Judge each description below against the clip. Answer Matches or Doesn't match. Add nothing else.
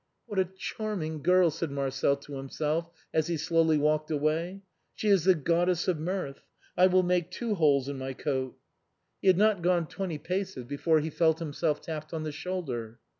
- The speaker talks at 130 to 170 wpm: Doesn't match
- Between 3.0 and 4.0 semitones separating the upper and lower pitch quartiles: Matches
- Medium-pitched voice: Matches